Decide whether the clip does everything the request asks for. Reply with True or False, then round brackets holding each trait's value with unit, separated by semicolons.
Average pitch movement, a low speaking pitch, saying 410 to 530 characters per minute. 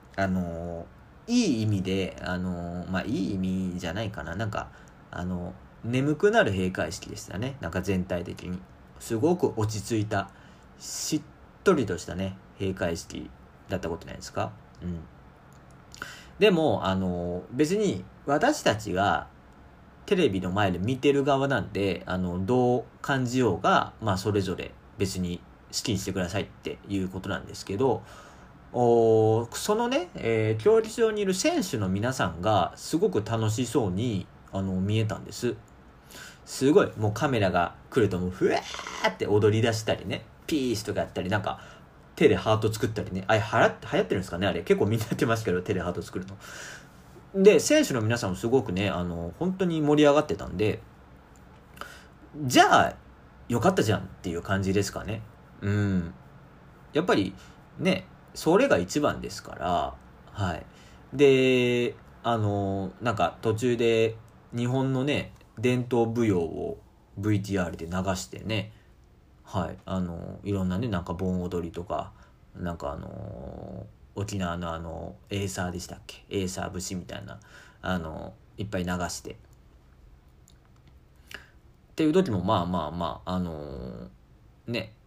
False (4.5 semitones; 95 Hz; 295 characters per minute)